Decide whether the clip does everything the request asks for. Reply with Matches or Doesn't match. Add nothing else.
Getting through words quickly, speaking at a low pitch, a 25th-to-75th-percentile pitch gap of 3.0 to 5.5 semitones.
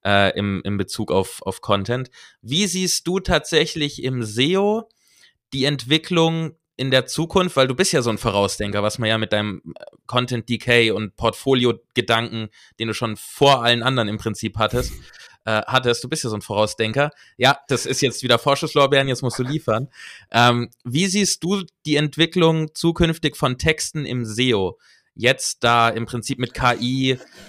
Doesn't match